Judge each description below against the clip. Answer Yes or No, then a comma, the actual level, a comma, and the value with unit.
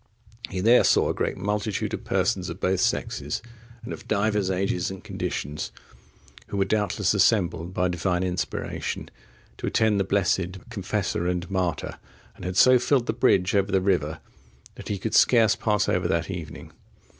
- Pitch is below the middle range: Yes, very low, 95 Hz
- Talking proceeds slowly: No, average, 170 wpm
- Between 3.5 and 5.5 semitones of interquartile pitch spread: No, average, 2.7 semitones